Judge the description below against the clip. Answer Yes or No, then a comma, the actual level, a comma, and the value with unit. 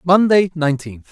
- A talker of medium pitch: Yes, medium, 160 Hz